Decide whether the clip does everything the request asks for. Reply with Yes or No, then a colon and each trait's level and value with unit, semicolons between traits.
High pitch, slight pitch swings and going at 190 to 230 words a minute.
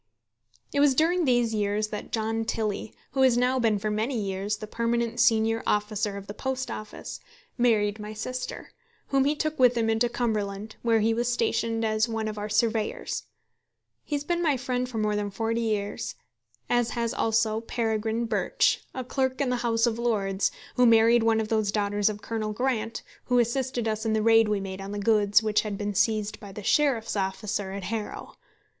Yes: high, 225 Hz; narrow, 2.3 semitones; average, 195 wpm